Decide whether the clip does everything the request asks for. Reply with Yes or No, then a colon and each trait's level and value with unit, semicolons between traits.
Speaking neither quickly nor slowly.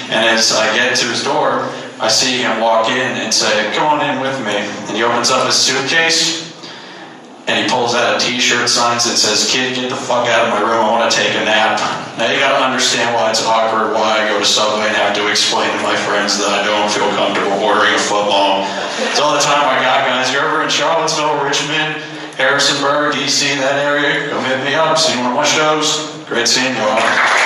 No: fast, 225 wpm